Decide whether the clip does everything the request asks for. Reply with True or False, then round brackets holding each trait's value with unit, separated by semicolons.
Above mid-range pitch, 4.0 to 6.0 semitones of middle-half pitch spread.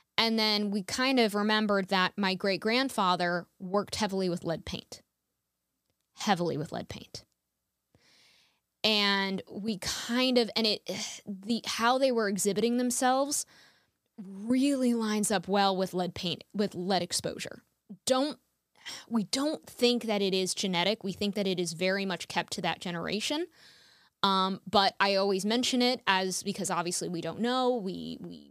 False (200 Hz; 3.6 semitones)